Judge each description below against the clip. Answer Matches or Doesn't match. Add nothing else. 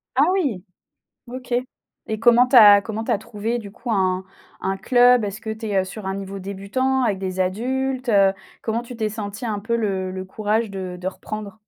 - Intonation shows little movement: Doesn't match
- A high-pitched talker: Matches